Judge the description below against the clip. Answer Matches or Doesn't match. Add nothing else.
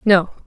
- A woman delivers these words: Matches